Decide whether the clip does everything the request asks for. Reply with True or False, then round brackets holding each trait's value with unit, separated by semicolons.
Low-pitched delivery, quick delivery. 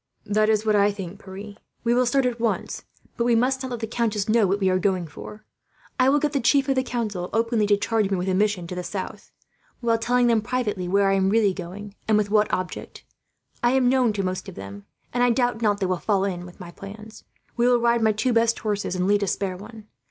False (210 Hz; 255 wpm)